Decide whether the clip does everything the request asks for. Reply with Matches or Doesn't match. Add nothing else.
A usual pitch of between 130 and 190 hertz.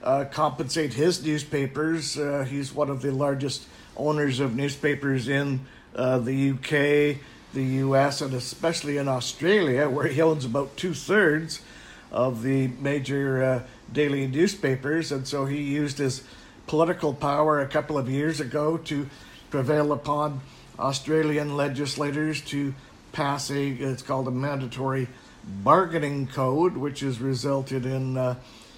Matches